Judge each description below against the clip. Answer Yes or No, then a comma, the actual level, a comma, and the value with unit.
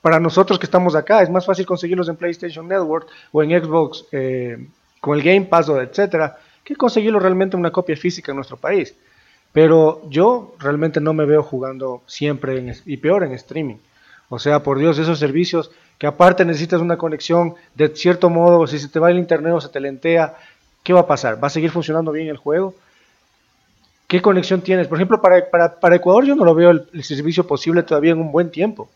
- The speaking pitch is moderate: Yes, medium, 165 Hz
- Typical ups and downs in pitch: Yes, average, 3.0 semitones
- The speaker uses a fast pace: Yes, fast, 210 wpm